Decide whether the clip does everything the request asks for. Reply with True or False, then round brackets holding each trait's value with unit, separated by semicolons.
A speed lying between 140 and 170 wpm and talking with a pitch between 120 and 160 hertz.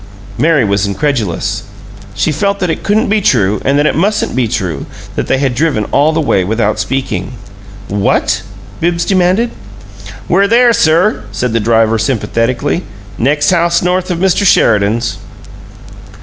True (150 wpm; 140 Hz)